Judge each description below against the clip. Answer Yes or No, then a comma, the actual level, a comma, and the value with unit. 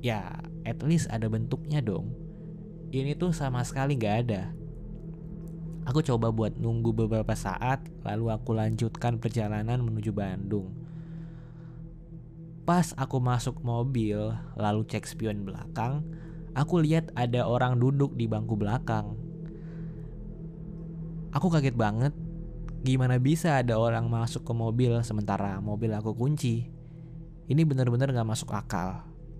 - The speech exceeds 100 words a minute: Yes, average, 120 wpm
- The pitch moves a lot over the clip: Yes, wide, 5.9 semitones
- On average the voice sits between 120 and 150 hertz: Yes, low, 135 Hz